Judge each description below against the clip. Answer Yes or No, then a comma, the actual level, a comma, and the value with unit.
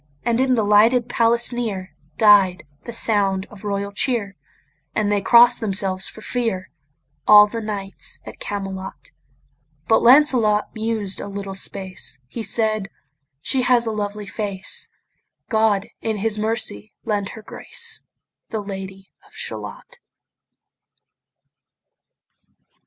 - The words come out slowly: Yes, slow, 125 wpm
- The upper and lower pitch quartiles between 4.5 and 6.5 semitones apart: No, average, 2.7 semitones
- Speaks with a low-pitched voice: No, high, 210 Hz